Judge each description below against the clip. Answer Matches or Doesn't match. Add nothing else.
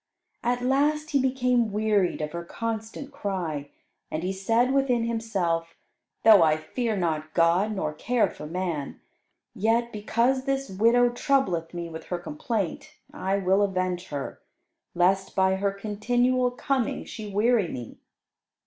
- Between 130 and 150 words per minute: Matches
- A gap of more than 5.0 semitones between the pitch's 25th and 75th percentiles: Matches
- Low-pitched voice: Doesn't match